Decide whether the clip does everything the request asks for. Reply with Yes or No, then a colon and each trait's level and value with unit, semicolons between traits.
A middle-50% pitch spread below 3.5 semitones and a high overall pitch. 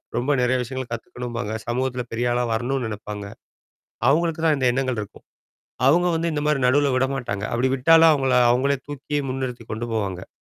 No: average, 2.9 semitones; low, 130 Hz